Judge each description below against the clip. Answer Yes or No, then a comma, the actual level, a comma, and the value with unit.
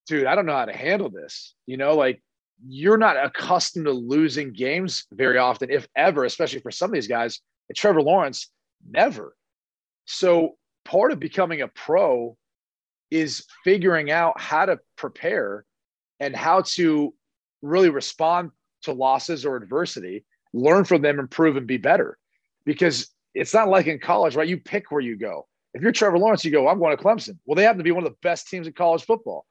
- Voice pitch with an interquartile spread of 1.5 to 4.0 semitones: No, average, 4.9 semitones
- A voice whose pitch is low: No, medium, 165 Hz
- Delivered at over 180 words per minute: Yes, average, 195 wpm